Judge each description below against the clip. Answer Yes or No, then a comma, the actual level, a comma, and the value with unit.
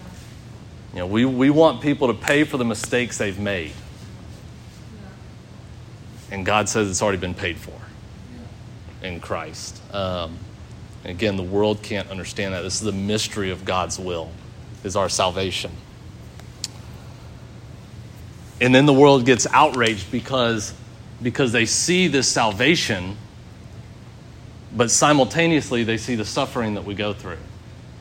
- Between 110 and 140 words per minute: Yes, slow, 135 wpm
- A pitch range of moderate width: Yes, average, 3.1 semitones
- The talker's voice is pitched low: Yes, low, 110 Hz